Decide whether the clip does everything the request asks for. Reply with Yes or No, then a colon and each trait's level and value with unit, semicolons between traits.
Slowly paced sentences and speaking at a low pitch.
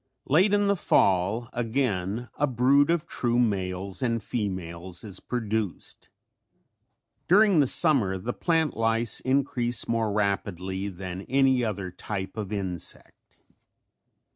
Yes: slow, 120 wpm; low, 115 Hz